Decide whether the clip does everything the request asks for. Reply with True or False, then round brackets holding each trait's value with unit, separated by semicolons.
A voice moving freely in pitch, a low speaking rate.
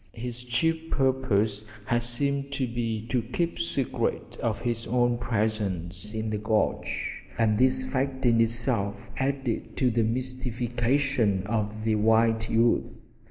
False (2.9 semitones; 130 wpm)